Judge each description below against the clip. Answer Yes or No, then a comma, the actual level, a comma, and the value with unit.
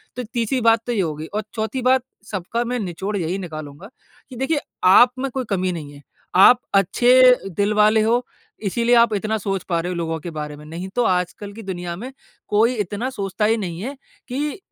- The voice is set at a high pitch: Yes, high, 210 Hz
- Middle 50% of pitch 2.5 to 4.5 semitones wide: No, average, 5.2 semitones